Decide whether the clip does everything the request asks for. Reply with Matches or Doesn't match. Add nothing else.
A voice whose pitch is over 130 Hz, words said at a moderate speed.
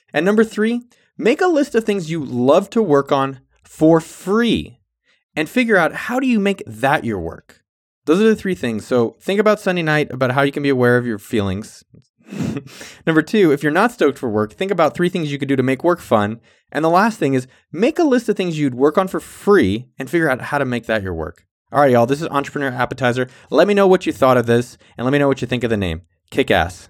Doesn't match